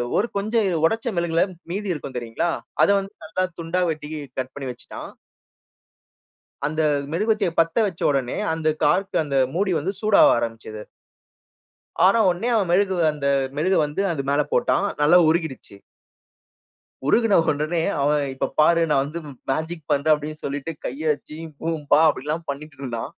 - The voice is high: No, medium, 160 Hz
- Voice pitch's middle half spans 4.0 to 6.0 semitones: Yes, average, 4.4 semitones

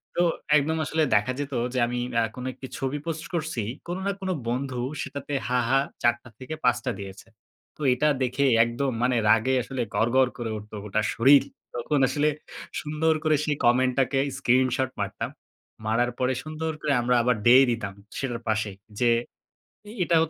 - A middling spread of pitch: Yes, average, 3.5 semitones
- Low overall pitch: Yes, low, 130 Hz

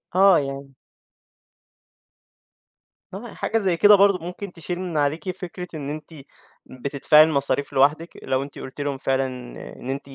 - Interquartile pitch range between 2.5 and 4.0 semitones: No, average, 4.7 semitones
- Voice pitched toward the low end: No, medium, 155 Hz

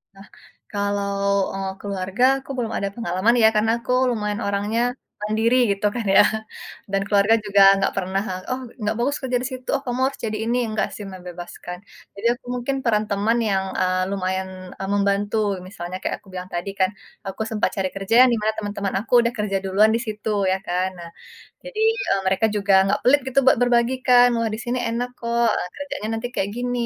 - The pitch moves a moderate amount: Yes, average, 3.3 semitones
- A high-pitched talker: Yes, high, 210 Hz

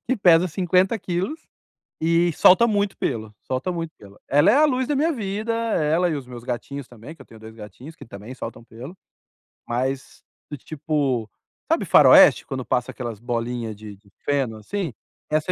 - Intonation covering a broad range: Yes, wide, 7.5 semitones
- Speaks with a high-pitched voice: No, medium, 145 Hz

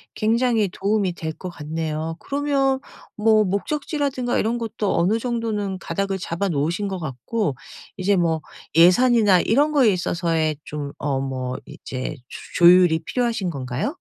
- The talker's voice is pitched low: No, high, 190 Hz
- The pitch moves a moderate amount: No, wide, 6.1 semitones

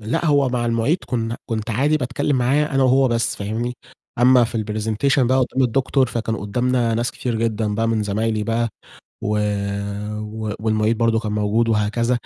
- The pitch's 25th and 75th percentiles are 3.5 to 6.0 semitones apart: No, narrow, 2.5 semitones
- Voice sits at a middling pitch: No, low, 115 Hz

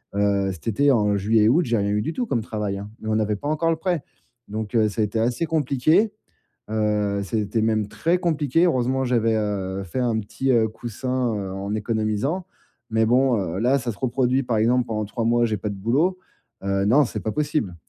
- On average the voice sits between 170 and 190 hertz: No, low, 115 Hz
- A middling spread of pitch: Yes, average, 4.1 semitones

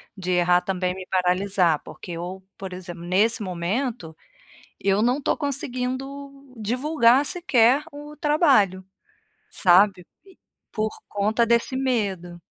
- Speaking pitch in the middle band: No, high, 210 Hz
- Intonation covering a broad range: Yes, wide, 6.1 semitones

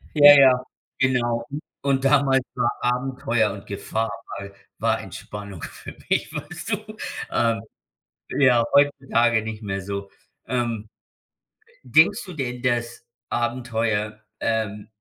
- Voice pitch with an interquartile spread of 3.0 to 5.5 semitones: Yes, average, 3.4 semitones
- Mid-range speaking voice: No, low, 120 Hz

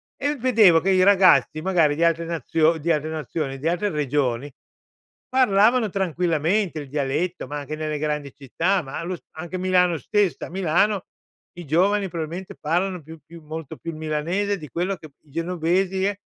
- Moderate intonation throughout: Yes, average, 3.6 semitones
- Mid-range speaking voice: Yes, medium, 170 Hz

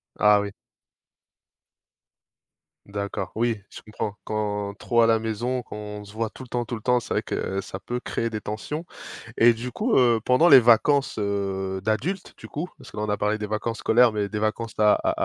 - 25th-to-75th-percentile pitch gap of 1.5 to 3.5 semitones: Yes, narrow, 2.5 semitones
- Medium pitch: No, low, 110 Hz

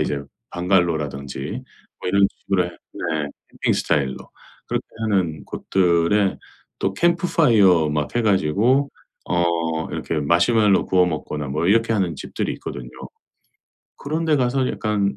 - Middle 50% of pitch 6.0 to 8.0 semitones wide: No, wide, 5.4 semitones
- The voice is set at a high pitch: No, very low, 90 Hz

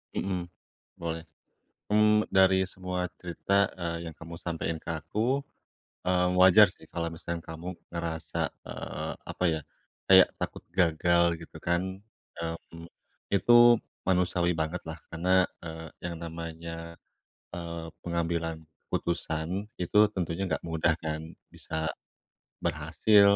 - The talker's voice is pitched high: No, very low, 85 Hz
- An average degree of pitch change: No, narrow, 1.8 semitones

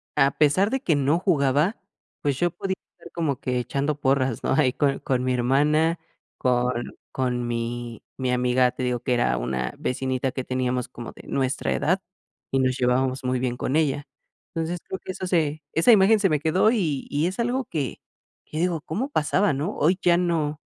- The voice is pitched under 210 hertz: Yes, medium, 140 Hz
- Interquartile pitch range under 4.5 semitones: No, average, 4.9 semitones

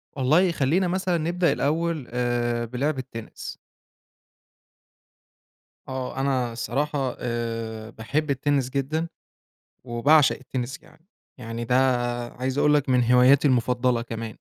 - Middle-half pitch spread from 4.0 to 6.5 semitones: No, average, 3.6 semitones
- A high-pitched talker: No, low, 130 Hz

